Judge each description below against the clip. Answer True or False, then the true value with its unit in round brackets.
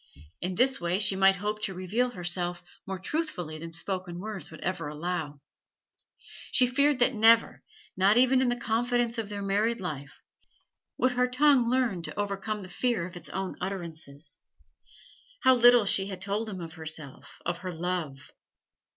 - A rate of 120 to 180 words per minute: True (170 wpm)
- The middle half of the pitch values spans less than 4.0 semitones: False (5.2 semitones)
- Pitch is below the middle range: False (195 Hz)